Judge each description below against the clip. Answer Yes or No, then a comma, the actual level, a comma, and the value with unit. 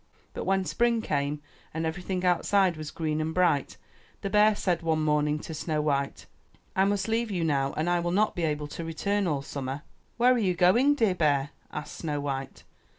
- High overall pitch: No, medium, 165 Hz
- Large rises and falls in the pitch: No, average, 4.4 semitones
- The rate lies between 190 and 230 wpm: Yes, average, 200 wpm